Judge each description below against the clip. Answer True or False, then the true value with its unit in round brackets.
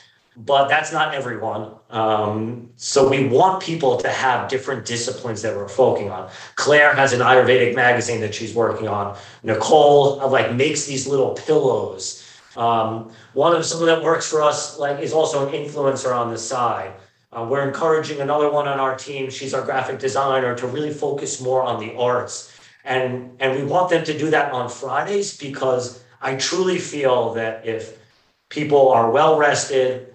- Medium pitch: False (130 Hz)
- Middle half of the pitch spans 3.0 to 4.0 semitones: True (3.7 semitones)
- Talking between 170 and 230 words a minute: True (175 wpm)